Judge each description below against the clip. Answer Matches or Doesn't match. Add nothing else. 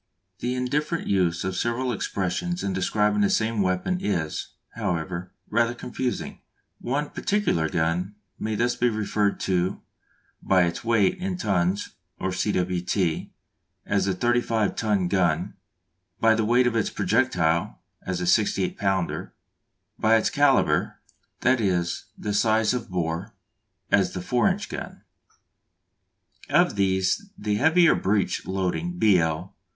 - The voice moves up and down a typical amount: Matches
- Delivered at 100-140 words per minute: Matches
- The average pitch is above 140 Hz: Doesn't match